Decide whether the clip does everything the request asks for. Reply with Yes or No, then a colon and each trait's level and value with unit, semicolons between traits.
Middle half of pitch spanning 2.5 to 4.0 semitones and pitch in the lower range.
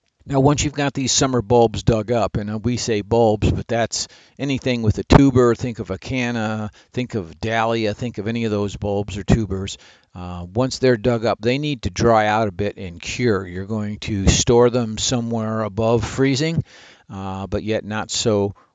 Yes: average, 3.1 semitones; low, 110 Hz